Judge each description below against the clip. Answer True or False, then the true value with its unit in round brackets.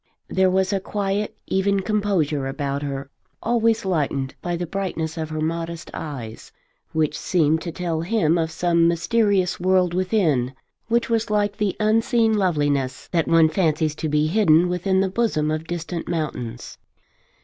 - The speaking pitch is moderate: True (170 Hz)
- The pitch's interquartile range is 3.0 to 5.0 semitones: True (4.2 semitones)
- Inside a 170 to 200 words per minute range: False (155 wpm)